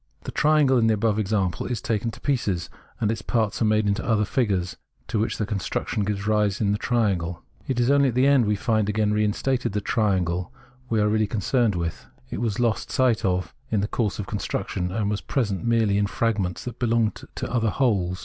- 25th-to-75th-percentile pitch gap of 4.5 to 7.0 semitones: No, narrow, 2.6 semitones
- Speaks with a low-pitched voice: Yes, low, 105 Hz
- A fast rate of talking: Yes, fast, 215 wpm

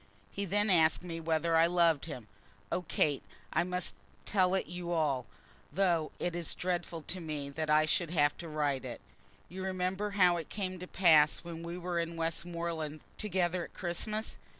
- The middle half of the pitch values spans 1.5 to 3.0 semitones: Yes, narrow, 2.4 semitones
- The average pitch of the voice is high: No, medium, 170 Hz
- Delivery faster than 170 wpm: Yes, average, 180 wpm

